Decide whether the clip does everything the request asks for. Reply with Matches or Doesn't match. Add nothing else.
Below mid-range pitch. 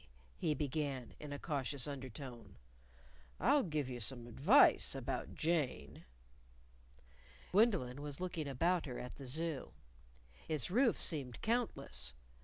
Doesn't match